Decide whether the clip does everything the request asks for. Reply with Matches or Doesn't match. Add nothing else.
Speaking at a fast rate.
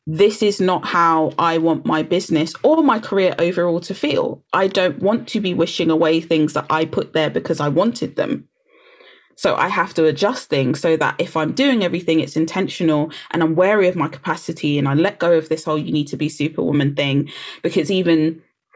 Matches